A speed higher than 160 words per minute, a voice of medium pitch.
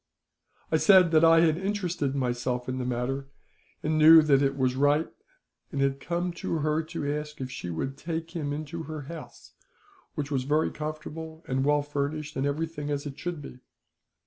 Yes: average, 195 wpm; medium, 150 Hz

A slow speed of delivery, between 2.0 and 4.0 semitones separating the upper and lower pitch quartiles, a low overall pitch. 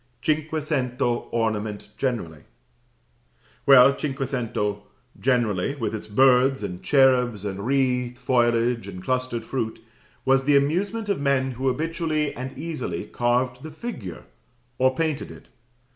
Yes: slow, 120 wpm; average, 3.2 semitones; low, 130 Hz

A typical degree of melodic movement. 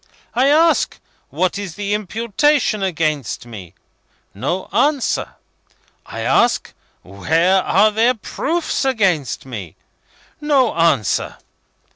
No: wide, 8.3 semitones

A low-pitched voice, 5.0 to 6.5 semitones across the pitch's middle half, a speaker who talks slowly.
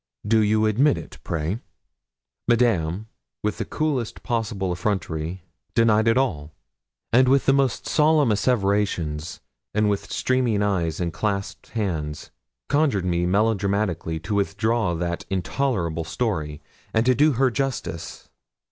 Yes: low, 105 Hz; wide, 5.5 semitones; slow, 125 wpm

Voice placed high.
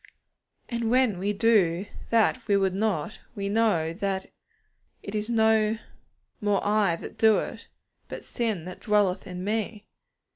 Yes: high, 210 Hz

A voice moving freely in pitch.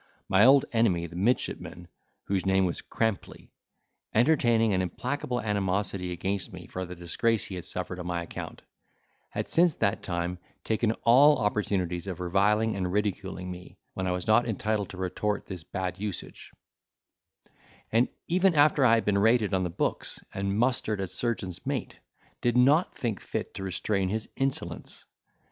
No: average, 3.9 semitones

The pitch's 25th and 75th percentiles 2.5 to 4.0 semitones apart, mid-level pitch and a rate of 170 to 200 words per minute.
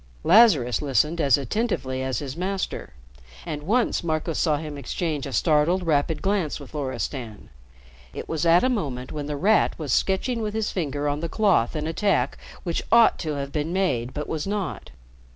No: average, 5.1 semitones; medium, 155 Hz; average, 180 wpm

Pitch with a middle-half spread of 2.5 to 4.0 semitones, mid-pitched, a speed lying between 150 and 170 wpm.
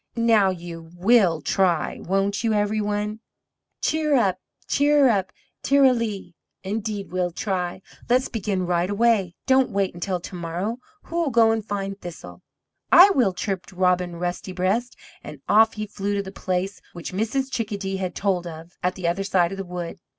No: average, 3.6 semitones; high, 195 Hz; average, 165 wpm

